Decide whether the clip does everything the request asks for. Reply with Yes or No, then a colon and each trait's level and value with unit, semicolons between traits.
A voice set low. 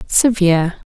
No: high, 190 Hz